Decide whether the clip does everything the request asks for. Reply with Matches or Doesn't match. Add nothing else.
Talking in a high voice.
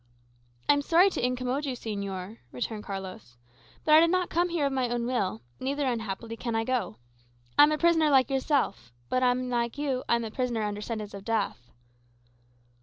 Matches